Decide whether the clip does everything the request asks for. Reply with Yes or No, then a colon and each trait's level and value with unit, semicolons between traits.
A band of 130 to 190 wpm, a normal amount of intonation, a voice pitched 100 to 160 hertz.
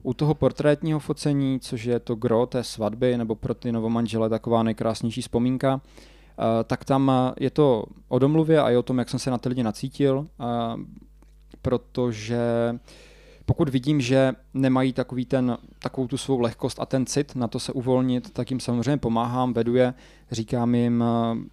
No: average, 165 wpm; narrow, 2.0 semitones; low, 125 Hz